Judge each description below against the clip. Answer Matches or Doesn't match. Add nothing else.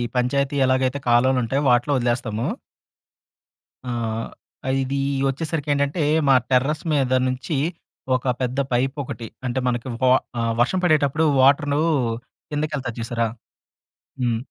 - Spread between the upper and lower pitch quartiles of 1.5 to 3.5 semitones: Matches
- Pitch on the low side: Matches